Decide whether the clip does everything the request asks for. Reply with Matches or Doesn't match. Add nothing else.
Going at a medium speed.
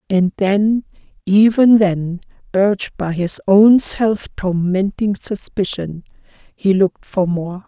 Doesn't match